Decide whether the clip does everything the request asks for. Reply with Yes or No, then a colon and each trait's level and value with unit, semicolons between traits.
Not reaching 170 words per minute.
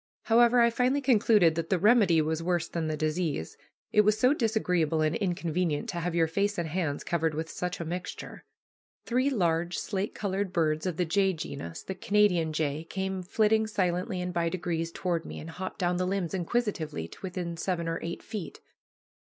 No: average, 190 wpm